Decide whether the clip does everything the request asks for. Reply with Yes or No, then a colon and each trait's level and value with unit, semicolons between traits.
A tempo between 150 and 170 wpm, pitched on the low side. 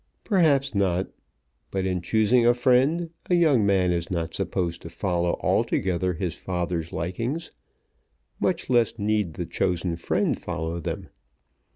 No: average, 140 wpm; very low, 95 Hz